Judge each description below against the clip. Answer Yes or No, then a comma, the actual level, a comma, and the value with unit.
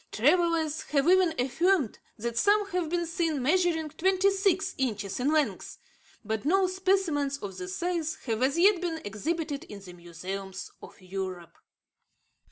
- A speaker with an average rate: Yes, average, 150 wpm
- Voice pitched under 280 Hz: No, very high, 310 Hz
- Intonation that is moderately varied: No, wide, 8.7 semitones